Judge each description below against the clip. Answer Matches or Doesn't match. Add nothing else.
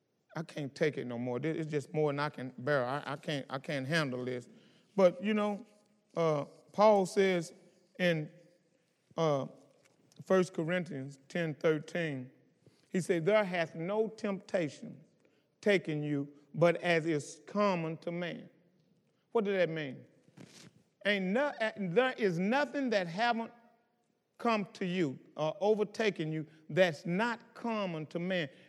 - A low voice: Doesn't match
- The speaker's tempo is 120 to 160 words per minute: Matches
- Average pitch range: Matches